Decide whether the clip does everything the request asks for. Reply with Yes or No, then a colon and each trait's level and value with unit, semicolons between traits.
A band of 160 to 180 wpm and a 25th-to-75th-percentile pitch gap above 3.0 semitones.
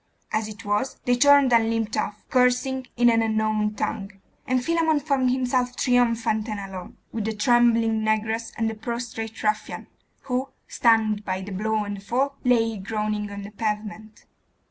No: average, 165 wpm; average, 2.7 semitones